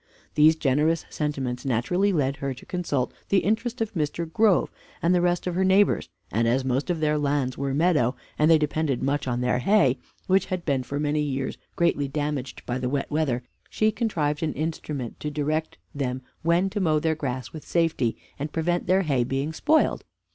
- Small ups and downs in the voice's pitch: No, average, 4.2 semitones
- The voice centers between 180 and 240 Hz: No, medium, 150 Hz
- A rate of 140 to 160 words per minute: No, average, 195 wpm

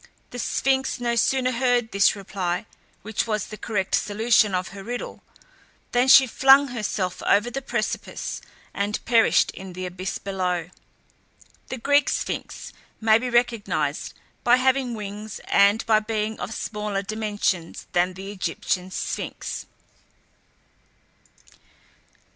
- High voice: Yes, high, 215 Hz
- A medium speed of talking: No, slow, 125 wpm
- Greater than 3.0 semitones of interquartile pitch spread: Yes, average, 3.9 semitones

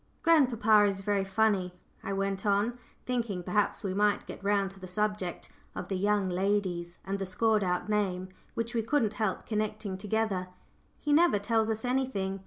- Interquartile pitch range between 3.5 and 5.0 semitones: No, narrow, 2.4 semitones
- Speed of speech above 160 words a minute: Yes, average, 175 wpm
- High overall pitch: Yes, high, 205 Hz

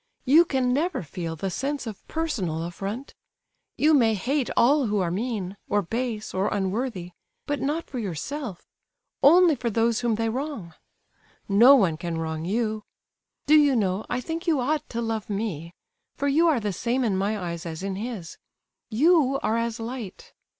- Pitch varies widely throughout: Yes, wide, 6.2 semitones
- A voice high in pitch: Yes, high, 230 Hz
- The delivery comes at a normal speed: Yes, average, 165 wpm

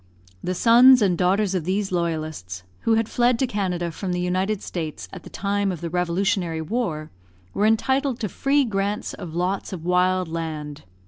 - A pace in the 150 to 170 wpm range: No, average, 180 wpm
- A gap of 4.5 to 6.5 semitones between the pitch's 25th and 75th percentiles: No, average, 3.7 semitones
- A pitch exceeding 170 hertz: Yes, medium, 185 Hz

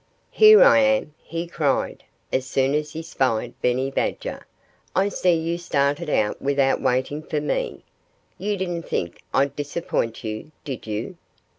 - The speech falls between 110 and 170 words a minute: Yes, average, 150 wpm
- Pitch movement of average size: Yes, average, 4.6 semitones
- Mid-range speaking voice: Yes, medium, 150 Hz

